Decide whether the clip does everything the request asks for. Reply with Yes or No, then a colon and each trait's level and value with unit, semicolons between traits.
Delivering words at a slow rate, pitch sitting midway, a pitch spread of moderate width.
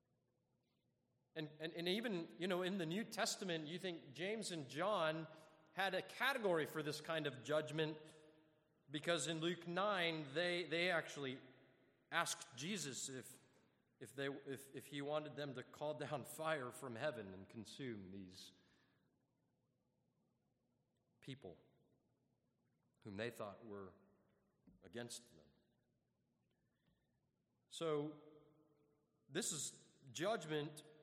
Yes: slow, 115 wpm; medium, 155 Hz; average, 4.3 semitones